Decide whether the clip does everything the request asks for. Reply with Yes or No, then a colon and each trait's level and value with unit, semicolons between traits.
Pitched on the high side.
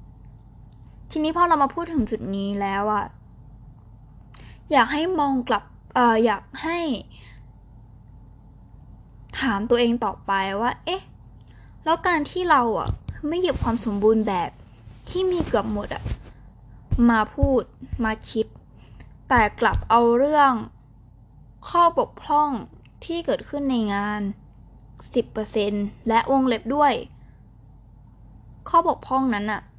Yes: high, 215 Hz